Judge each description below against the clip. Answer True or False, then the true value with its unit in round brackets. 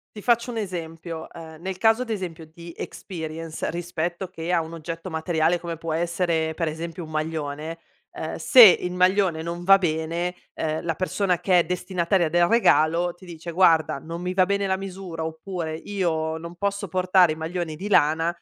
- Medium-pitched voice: True (170 Hz)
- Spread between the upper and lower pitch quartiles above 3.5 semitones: False (2.4 semitones)